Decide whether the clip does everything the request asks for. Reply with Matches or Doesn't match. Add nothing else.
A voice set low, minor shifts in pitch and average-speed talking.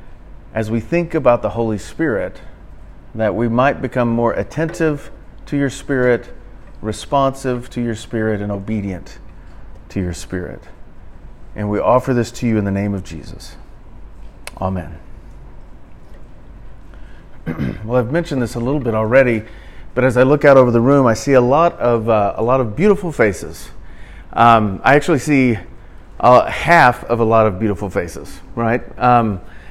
Doesn't match